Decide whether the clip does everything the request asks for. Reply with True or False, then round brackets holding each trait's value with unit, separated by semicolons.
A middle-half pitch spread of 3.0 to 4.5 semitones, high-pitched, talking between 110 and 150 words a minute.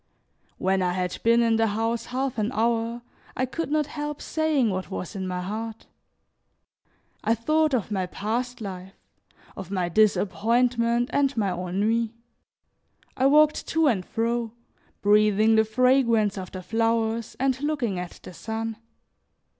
True (3.6 semitones; 225 Hz; 145 wpm)